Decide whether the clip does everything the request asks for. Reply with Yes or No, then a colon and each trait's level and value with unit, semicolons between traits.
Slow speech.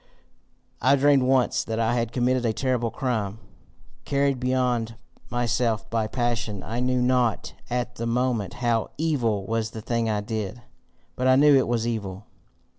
No: average, 160 wpm